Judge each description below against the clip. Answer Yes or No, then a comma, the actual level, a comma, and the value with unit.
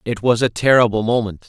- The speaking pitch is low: Yes, low, 115 Hz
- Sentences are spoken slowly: No, fast, 205 wpm